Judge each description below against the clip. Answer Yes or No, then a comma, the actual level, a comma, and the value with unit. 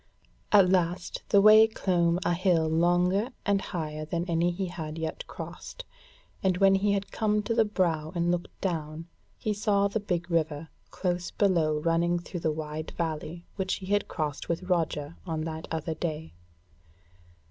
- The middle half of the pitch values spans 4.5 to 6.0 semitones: No, average, 3.3 semitones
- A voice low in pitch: No, medium, 175 Hz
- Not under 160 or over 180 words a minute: Yes, average, 170 wpm